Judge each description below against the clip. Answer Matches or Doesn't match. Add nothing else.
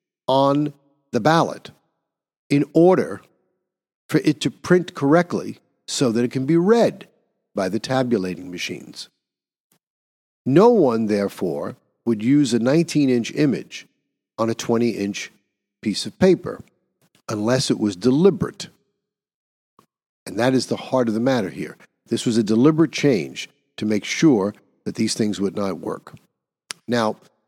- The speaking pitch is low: Matches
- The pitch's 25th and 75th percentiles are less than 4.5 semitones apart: Doesn't match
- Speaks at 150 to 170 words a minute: Doesn't match